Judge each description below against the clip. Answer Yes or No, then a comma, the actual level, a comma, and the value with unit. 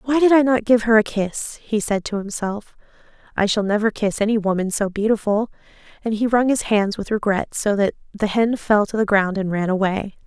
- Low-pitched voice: No, high, 210 Hz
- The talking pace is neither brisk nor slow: No, fast, 220 wpm